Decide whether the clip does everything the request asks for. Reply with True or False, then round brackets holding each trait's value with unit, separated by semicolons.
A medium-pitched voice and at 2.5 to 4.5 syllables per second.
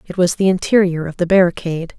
False (180 Hz; 6.4 syllables/s)